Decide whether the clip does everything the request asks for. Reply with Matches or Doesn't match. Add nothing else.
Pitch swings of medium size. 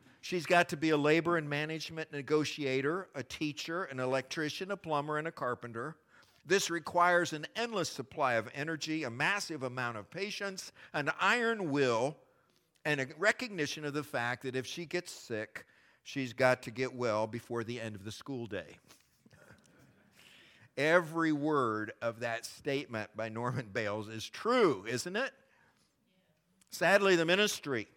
Doesn't match